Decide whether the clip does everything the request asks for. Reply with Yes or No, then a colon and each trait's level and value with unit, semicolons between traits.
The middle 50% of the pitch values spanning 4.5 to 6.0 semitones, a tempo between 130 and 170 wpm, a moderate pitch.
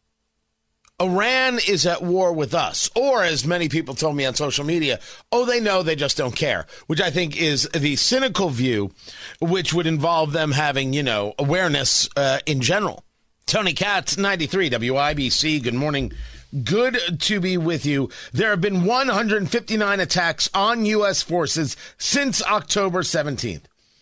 Yes: wide, 5.4 semitones; average, 155 wpm; medium, 165 Hz